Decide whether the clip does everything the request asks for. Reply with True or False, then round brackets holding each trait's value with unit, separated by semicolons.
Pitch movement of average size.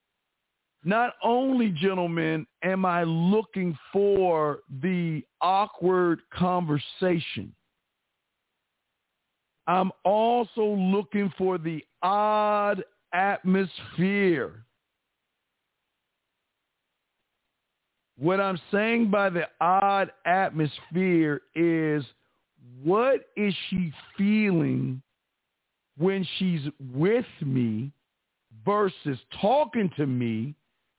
True (4.9 semitones)